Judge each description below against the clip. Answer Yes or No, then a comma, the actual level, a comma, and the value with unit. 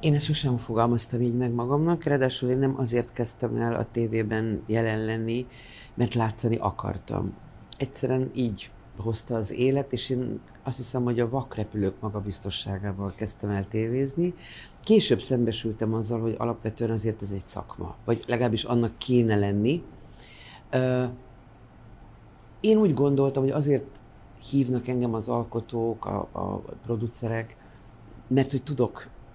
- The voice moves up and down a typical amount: No, narrow, 2.2 semitones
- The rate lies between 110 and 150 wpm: Yes, slow, 135 wpm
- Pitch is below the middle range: Yes, low, 115 Hz